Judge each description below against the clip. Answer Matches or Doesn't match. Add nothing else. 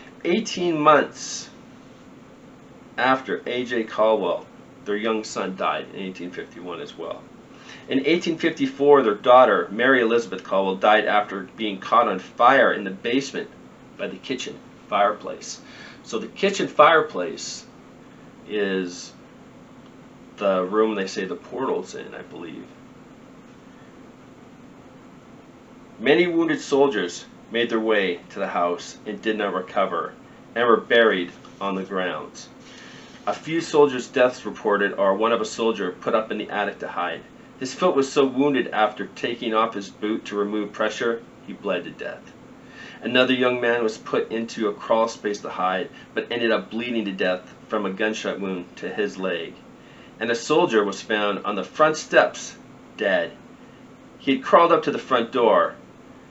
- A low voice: Matches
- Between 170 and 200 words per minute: Doesn't match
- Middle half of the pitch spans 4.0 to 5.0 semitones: Matches